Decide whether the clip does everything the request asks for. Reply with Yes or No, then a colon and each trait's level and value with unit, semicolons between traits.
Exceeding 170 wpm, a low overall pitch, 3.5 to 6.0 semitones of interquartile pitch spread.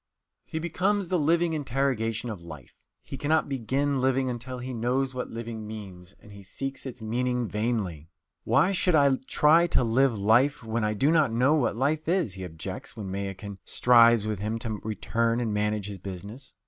Yes: average, 185 wpm; low, 120 Hz; average, 4.4 semitones